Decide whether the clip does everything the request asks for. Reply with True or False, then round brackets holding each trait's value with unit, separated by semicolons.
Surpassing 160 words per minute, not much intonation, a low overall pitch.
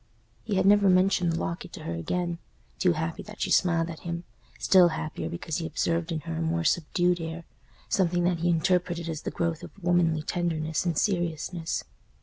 False (185 wpm; 1.6 semitones; 170 Hz)